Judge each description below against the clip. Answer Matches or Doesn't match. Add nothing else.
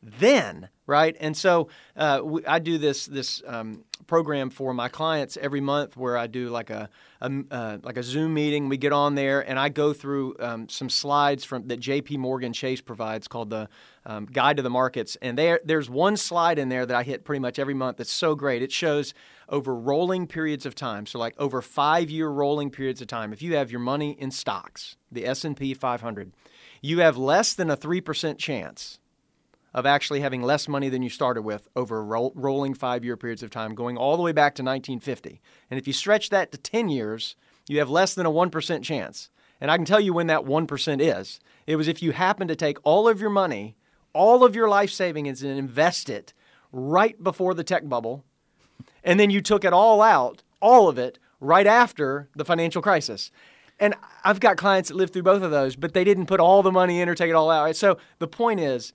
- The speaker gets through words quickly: Matches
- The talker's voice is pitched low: Doesn't match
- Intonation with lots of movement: Doesn't match